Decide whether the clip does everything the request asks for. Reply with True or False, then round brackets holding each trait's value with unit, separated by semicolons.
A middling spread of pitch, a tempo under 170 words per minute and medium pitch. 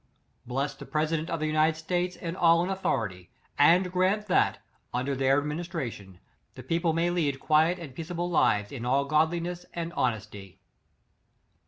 True (4.4 semitones; 160 wpm; 160 Hz)